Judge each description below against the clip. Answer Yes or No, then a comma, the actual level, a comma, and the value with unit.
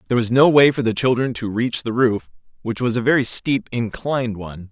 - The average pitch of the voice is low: Yes, low, 120 Hz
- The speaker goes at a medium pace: No, fast, 230 wpm